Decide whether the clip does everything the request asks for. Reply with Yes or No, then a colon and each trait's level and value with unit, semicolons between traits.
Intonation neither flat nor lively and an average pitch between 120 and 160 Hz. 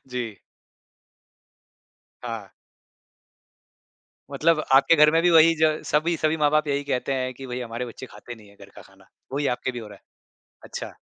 Yes: average, 4.0 semitones; low, 135 Hz